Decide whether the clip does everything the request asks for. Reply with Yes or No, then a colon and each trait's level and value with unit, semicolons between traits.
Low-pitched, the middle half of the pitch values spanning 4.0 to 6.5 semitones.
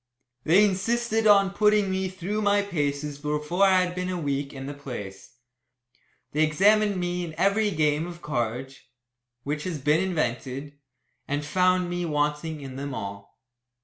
No: medium, 160 Hz; average, 4.8 semitones